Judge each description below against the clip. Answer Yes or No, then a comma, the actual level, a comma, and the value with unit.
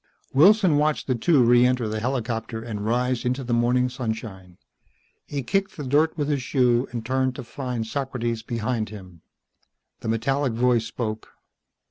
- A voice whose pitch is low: Yes, low, 125 Hz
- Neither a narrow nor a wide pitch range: Yes, average, 3.0 semitones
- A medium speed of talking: Yes, average, 160 wpm